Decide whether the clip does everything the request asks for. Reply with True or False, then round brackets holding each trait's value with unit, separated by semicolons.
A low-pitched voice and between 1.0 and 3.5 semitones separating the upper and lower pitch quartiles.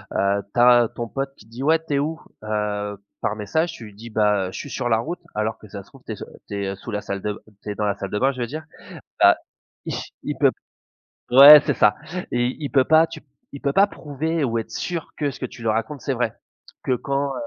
False (120 Hz; 5.3 semitones)